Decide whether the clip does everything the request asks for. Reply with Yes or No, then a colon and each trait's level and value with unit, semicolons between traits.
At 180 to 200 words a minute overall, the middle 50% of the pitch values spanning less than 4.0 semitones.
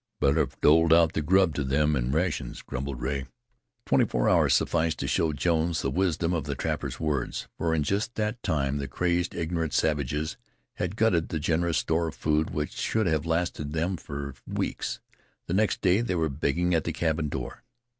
Yes: average, 195 wpm; average, 2.9 semitones